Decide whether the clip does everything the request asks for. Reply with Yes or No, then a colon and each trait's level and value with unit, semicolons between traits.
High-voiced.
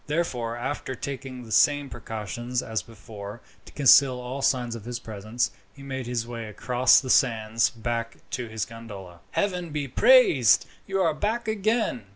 No: low, 125 Hz